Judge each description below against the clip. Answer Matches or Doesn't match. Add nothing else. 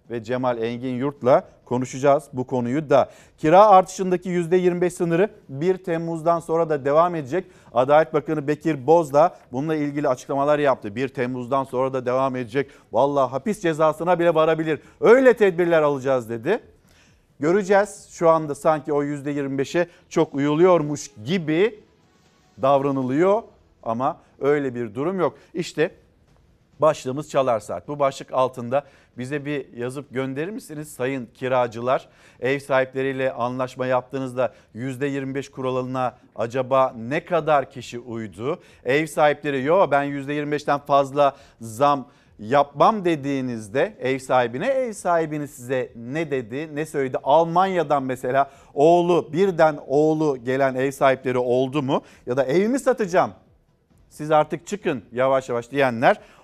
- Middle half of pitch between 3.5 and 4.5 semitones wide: Matches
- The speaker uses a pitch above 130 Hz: Matches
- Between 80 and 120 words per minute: Doesn't match